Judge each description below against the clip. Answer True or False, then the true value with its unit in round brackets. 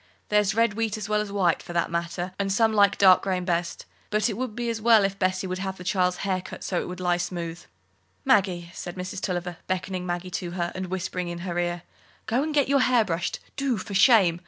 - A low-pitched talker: False (185 Hz)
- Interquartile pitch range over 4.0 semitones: False (3.2 semitones)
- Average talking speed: False (240 wpm)